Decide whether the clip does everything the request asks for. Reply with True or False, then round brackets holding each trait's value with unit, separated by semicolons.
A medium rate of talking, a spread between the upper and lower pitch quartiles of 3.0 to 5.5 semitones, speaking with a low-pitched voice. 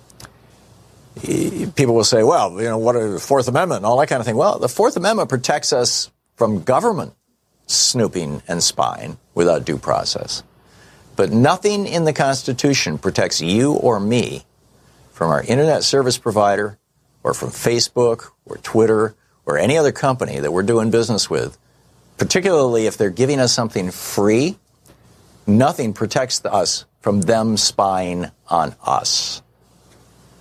True (145 wpm; 3.8 semitones; 115 Hz)